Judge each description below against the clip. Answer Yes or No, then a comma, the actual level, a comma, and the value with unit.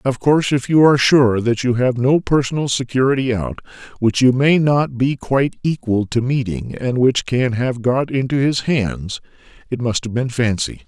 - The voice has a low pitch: Yes, low, 125 Hz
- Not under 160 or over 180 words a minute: No, average, 195 wpm